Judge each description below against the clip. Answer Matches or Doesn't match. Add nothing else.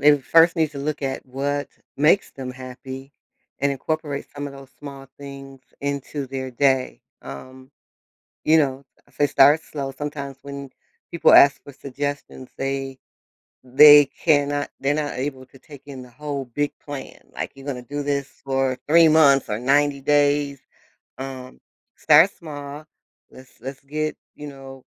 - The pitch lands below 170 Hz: Matches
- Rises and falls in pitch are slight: Matches